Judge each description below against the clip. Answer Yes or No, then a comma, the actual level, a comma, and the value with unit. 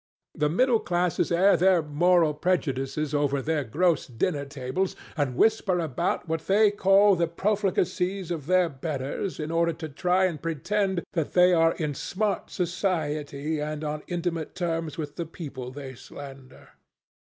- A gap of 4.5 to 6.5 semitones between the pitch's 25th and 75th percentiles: No, average, 3.7 semitones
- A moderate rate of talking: Yes, average, 150 wpm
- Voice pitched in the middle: Yes, medium, 165 Hz